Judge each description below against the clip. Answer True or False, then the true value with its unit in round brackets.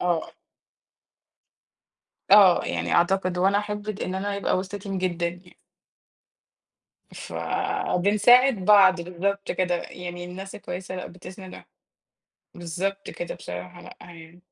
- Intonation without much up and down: True (2.1 semitones)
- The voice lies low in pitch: False (185 Hz)